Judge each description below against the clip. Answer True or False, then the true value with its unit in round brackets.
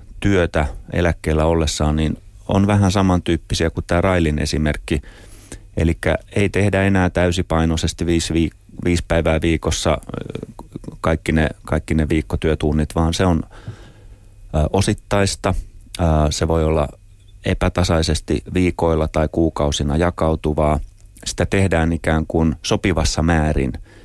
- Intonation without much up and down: False (3.5 semitones)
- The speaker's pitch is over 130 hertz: False (85 Hz)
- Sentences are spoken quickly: False (110 wpm)